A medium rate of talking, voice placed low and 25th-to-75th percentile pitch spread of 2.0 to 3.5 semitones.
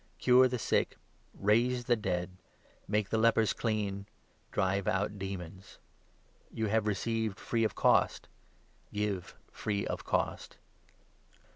No: slow, 125 wpm; low, 105 Hz; narrow, 2.5 semitones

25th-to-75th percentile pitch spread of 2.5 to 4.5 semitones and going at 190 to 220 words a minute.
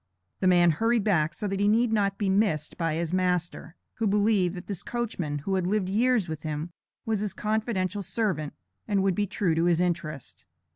Yes: average, 3.7 semitones; average, 200 wpm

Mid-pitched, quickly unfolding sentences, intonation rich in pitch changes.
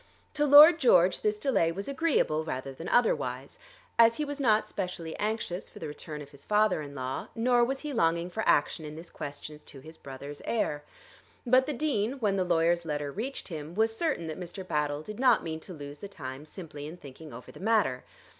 Yes: medium, 175 Hz; fast, 210 wpm; wide, 7.3 semitones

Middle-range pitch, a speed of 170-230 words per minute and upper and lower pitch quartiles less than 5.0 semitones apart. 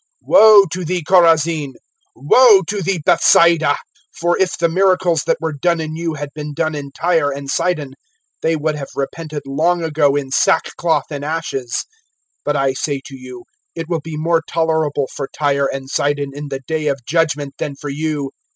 Yes: medium, 155 Hz; average, 180 wpm; average, 2.8 semitones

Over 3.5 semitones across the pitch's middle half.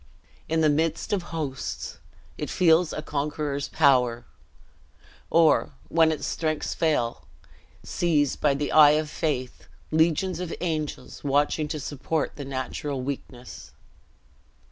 No: narrow, 2.4 semitones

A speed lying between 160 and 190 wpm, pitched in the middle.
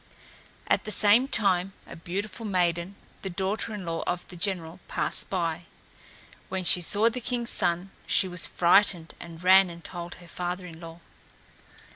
Yes: average, 165 wpm; medium, 180 Hz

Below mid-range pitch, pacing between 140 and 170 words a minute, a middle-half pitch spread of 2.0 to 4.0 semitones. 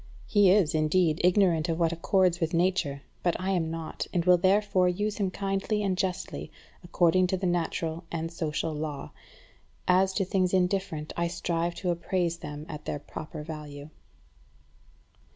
No: medium, 175 Hz; average, 160 wpm; narrow, 2.6 semitones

